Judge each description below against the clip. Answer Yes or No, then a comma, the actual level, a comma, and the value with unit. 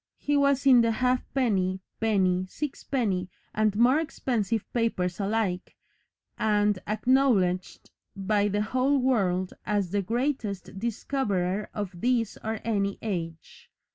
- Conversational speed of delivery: No, slow, 120 wpm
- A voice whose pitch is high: Yes, high, 215 Hz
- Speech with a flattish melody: No, average, 4.6 semitones